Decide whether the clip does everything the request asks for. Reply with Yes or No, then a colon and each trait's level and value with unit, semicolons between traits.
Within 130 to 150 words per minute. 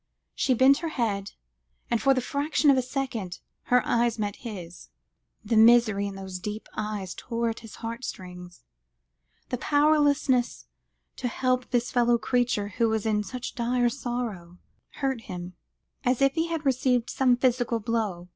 No: average, 160 wpm